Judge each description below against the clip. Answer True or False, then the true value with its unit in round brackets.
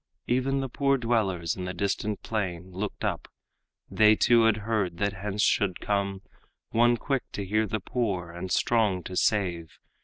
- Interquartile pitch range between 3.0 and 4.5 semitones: True (3.6 semitones)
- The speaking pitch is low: True (105 Hz)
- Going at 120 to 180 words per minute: True (165 wpm)